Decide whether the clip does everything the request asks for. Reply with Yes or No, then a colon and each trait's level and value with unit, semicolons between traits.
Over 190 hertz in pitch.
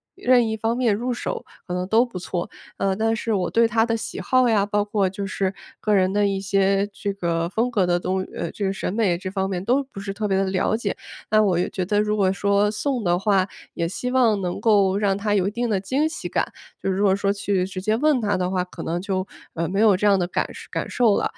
Yes: high, 200 Hz